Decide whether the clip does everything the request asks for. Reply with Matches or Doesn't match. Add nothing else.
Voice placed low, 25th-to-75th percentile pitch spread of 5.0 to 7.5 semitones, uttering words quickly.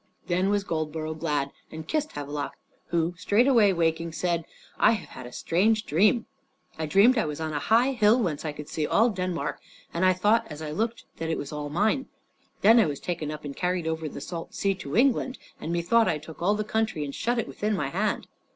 Doesn't match